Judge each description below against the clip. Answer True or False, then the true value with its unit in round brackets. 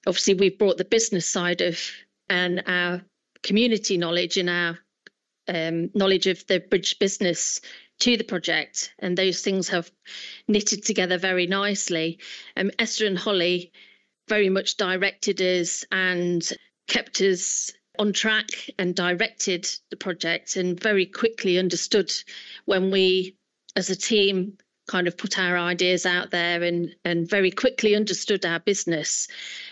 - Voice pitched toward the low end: False (185 Hz)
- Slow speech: False (145 wpm)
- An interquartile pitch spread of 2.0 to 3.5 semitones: True (2.4 semitones)